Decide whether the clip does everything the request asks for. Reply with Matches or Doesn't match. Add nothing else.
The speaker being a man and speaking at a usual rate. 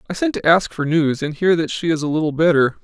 Doesn't match